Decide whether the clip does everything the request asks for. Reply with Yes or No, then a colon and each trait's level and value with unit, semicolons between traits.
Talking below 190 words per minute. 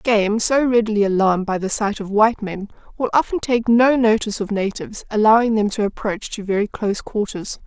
No: average, 195 wpm